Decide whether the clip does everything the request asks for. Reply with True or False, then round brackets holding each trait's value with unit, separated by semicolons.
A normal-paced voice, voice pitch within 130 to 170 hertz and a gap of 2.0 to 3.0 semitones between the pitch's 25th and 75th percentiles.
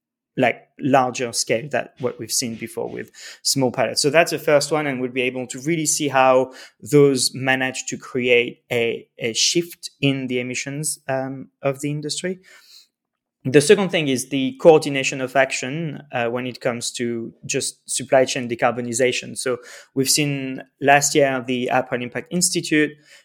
True (165 wpm; 135 Hz; 2.5 semitones)